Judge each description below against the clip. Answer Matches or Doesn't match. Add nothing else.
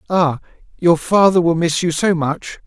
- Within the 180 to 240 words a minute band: Doesn't match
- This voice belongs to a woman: Doesn't match